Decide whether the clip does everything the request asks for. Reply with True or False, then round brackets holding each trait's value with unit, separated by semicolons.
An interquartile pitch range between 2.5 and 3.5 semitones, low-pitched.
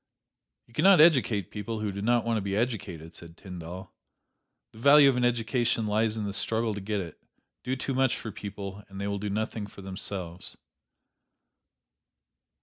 True (3.1 semitones; 105 Hz)